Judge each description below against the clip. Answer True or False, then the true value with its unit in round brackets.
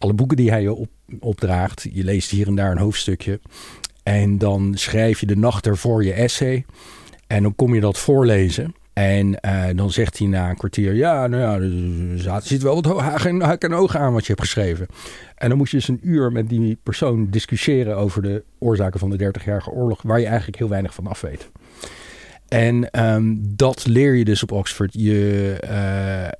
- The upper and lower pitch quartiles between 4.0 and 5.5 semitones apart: False (3.4 semitones)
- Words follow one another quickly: True (205 wpm)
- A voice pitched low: True (105 Hz)